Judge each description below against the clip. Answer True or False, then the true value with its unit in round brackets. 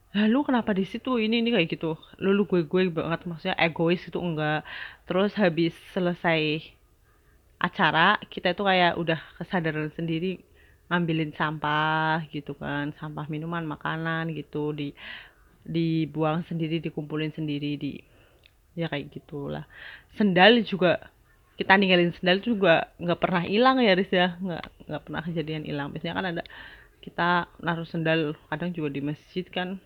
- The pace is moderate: False (145 wpm)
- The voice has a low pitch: False (165 Hz)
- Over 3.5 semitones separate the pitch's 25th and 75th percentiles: False (3.1 semitones)